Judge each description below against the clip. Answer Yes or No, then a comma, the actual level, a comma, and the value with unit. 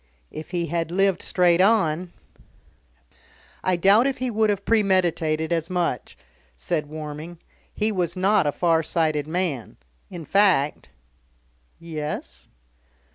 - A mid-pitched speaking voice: Yes, medium, 170 Hz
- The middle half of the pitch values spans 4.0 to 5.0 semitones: No, average, 3.6 semitones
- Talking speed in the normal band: No, slow, 130 wpm